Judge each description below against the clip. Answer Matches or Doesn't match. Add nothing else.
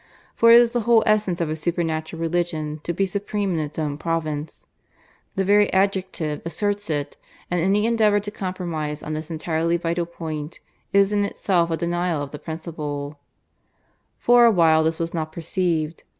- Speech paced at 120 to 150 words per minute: Doesn't match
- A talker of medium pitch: Matches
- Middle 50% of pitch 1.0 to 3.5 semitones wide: Doesn't match